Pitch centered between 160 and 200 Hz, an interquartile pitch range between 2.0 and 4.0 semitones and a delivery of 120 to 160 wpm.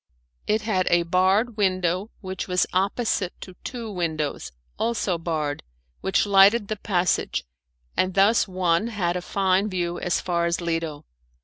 Yes: medium, 185 Hz; average, 2.8 semitones; average, 145 wpm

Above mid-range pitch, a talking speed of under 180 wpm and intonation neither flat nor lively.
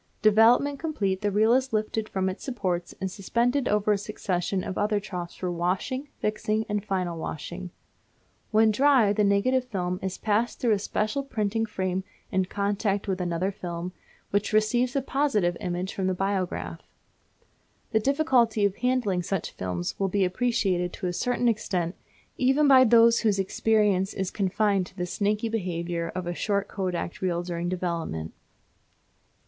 Yes: high, 200 Hz; average, 160 wpm; average, 3.5 semitones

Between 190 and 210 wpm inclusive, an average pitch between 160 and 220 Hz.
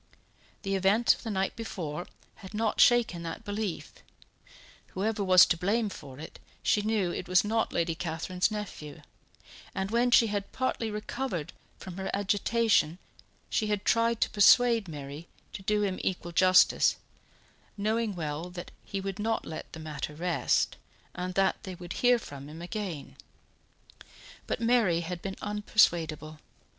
No: average, 150 wpm; high, 190 Hz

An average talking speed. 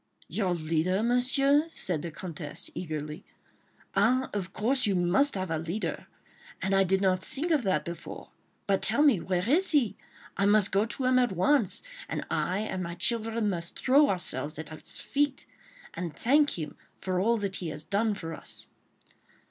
Yes: average, 180 wpm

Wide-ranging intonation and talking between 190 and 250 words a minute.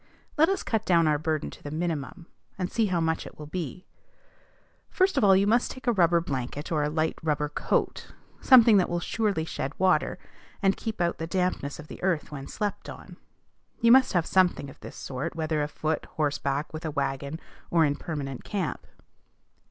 No: average, 4.4 semitones; average, 195 wpm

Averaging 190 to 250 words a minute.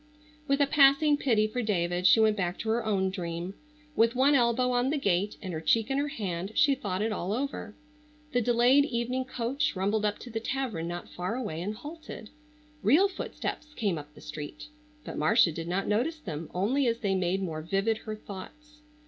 Yes: average, 200 wpm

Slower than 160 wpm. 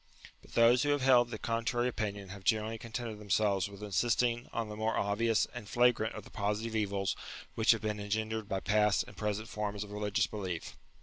No: fast, 205 wpm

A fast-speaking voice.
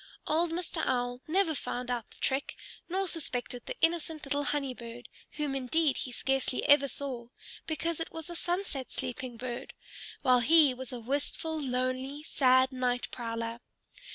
No: average, 155 wpm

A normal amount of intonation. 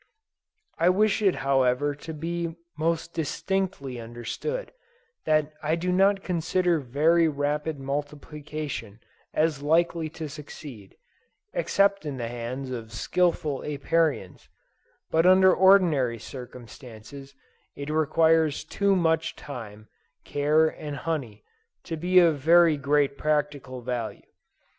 Yes: average, 3.6 semitones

